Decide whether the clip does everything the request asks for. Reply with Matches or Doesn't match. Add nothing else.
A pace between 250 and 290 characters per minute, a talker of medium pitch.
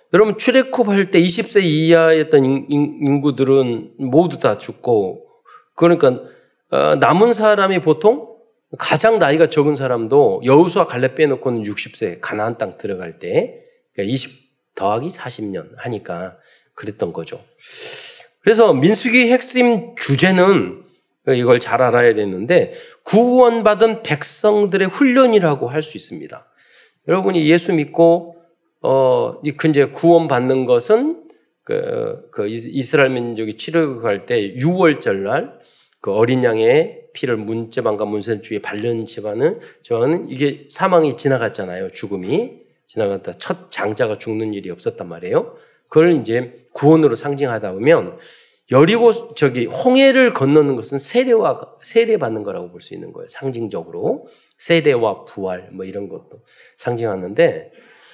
Matches